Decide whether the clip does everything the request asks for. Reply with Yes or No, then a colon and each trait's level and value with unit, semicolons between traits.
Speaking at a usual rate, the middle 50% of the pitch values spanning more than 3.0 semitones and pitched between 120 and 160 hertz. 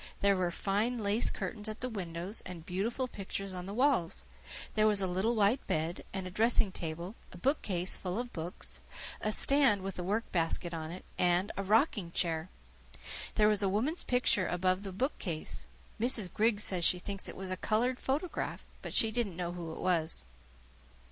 No: average, 190 wpm; average, 3.8 semitones; high, 195 Hz